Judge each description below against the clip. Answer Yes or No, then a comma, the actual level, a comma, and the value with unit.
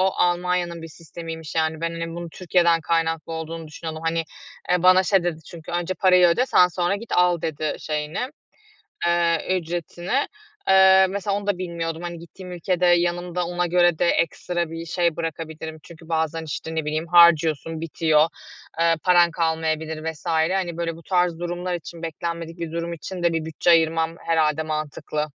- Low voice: No, medium, 170 Hz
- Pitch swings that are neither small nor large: No, narrow, 1.5 semitones